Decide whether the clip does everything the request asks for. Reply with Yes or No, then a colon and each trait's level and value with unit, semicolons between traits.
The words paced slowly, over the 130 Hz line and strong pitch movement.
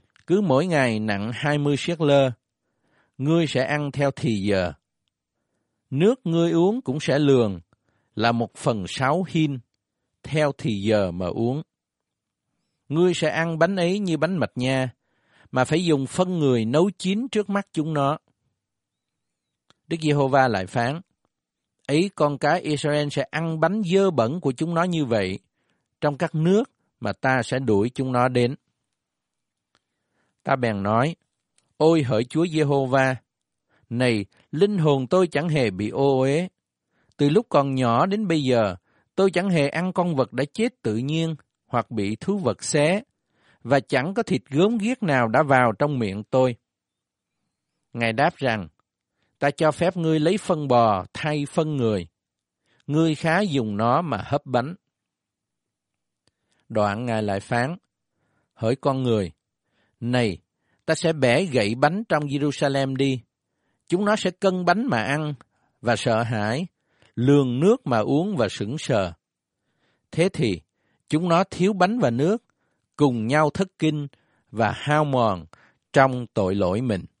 Yes: slow, 155 wpm; medium, 140 Hz; wide, 5.9 semitones